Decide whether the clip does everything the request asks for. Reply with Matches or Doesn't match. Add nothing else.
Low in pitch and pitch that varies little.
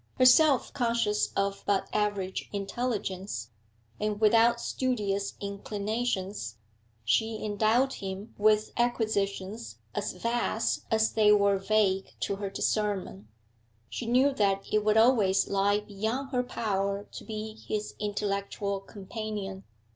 Doesn't match